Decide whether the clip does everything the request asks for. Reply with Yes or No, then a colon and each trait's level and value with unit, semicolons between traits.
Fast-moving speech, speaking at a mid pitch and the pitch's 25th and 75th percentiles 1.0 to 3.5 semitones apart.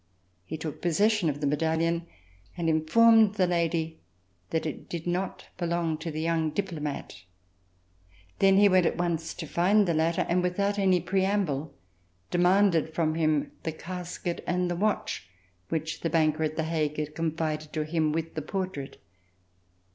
No: average, 160 wpm; medium, 165 Hz; narrow, 2.5 semitones